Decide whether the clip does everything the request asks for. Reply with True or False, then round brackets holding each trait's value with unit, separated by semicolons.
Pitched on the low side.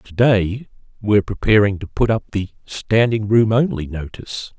True (105 Hz)